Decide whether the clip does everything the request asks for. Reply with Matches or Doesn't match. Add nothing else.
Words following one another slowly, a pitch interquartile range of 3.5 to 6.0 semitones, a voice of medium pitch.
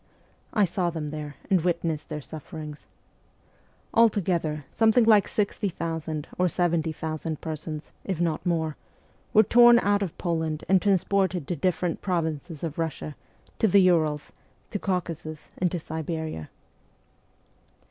Doesn't match